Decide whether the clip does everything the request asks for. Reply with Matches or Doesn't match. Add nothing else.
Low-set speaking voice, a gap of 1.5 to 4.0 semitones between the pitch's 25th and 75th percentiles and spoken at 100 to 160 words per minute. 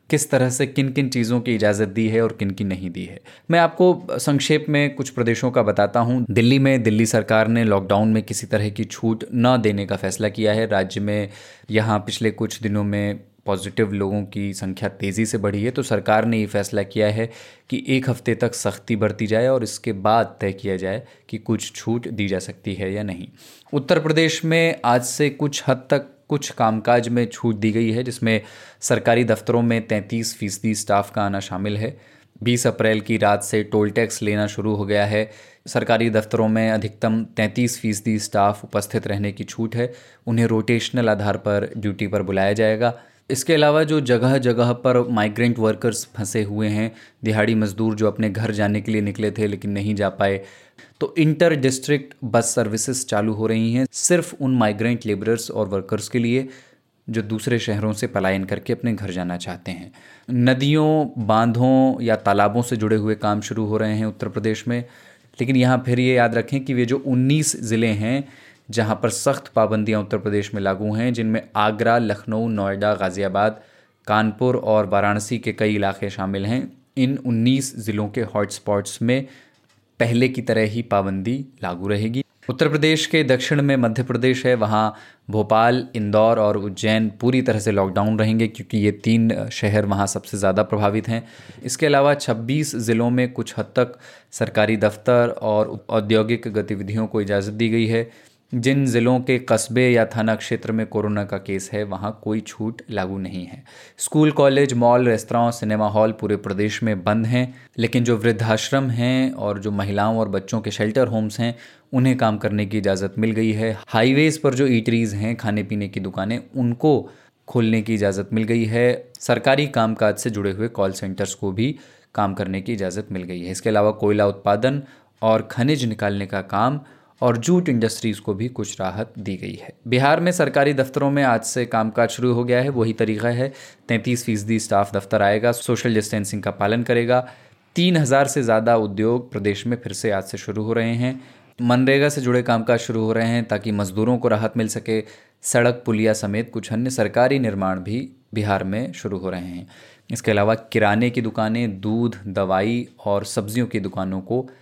Doesn't match